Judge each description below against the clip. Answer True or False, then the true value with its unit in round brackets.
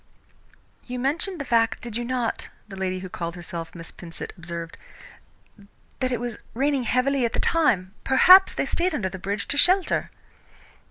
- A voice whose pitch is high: True (235 Hz)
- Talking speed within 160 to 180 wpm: True (170 wpm)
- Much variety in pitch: True (6.9 semitones)